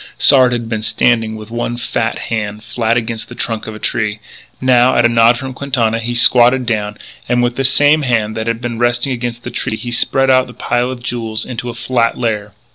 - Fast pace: Yes, fast, 220 wpm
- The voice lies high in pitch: No, low, 120 Hz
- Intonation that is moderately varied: No, narrow, 1.6 semitones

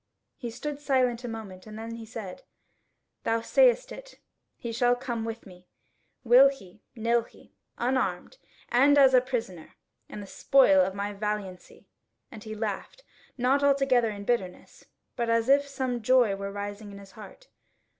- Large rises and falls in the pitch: No, average, 4.1 semitones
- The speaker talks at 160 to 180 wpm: Yes, average, 165 wpm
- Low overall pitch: No, high, 230 Hz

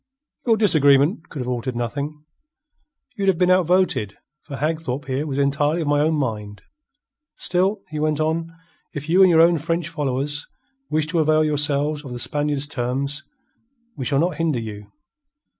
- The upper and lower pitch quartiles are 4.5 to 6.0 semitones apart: No, average, 3.1 semitones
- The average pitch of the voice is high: No, medium, 150 Hz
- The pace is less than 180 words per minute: Yes, average, 165 wpm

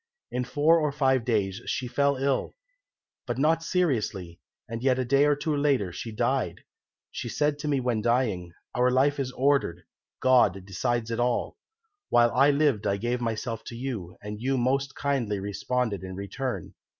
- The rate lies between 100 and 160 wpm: No, average, 175 wpm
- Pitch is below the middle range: Yes, low, 125 Hz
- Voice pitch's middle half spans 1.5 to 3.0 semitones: No, average, 4.3 semitones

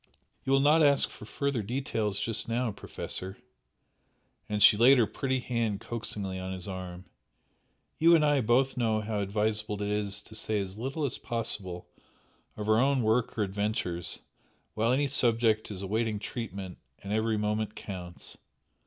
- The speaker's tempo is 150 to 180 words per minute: Yes, average, 160 wpm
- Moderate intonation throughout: Yes, average, 3.3 semitones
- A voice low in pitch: Yes, low, 110 Hz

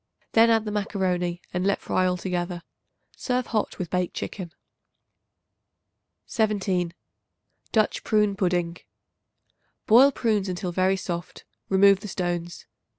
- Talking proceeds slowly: Yes, slow, 115 wpm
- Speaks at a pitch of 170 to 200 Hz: Yes, high, 190 Hz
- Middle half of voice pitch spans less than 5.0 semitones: Yes, average, 3.0 semitones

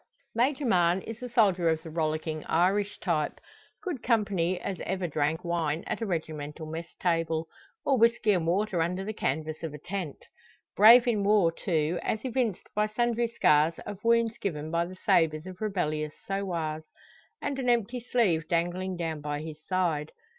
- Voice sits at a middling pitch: Yes, medium, 180 Hz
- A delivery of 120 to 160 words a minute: No, average, 170 wpm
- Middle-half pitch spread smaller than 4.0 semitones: No, average, 5.1 semitones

